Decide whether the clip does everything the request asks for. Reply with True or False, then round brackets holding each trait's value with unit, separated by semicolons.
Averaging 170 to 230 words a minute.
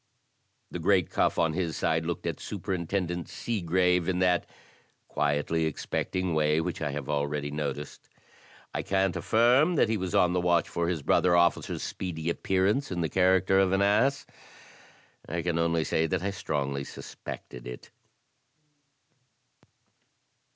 False (150 wpm)